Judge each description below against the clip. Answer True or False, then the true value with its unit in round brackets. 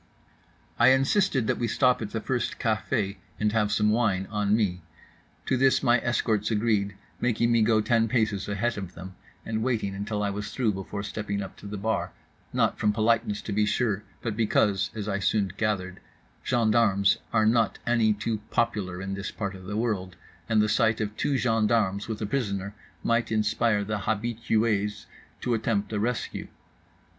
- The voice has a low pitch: True (105 Hz)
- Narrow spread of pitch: True (2.2 semitones)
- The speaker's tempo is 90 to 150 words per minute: False (175 wpm)